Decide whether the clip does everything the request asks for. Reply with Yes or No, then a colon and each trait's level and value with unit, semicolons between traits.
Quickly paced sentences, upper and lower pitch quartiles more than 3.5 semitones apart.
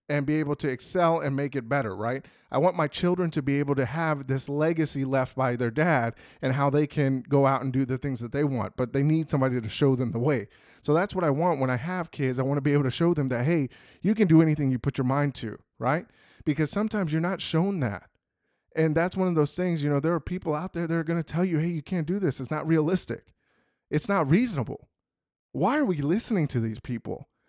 Yes: fast, 255 wpm; average, 3.9 semitones